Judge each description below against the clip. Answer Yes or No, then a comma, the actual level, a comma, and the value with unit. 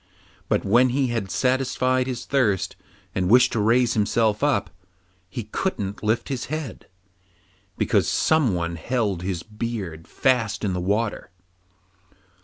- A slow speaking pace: Yes, slow, 130 wpm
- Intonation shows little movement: No, average, 4.4 semitones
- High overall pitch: No, low, 115 Hz